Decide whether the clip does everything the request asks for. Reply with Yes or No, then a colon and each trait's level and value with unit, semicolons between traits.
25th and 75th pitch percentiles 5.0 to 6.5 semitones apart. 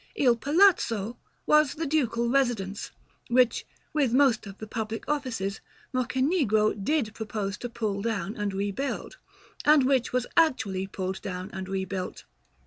Yes: wide, 5.4 semitones